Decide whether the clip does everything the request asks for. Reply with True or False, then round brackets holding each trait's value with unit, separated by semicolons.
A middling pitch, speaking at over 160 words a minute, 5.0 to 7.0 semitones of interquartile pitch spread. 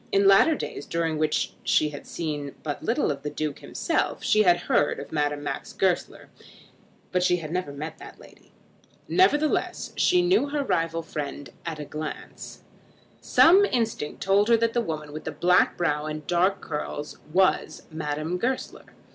True (165 Hz; 170 wpm; 5.4 semitones)